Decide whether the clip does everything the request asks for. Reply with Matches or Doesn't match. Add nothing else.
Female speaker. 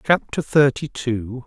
Doesn't match